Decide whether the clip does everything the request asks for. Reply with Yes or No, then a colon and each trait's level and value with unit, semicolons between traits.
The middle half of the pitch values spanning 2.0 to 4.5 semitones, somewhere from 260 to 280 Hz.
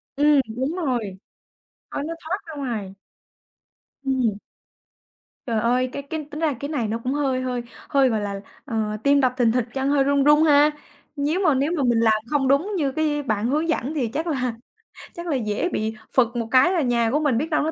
Yes: average, 3.9 semitones; very high, 270 Hz